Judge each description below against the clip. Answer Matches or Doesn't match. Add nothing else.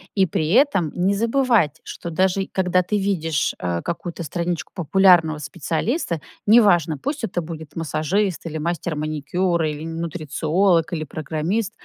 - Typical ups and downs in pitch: Matches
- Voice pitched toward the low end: Doesn't match